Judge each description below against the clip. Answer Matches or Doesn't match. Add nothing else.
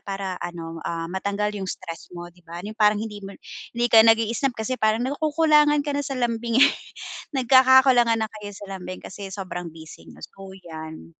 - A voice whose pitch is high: Matches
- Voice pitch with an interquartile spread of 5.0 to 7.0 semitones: Matches